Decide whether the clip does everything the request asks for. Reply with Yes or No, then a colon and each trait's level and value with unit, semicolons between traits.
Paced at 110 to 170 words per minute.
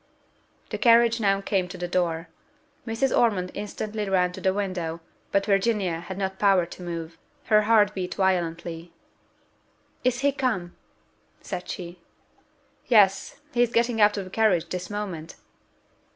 Yes: average, 150 wpm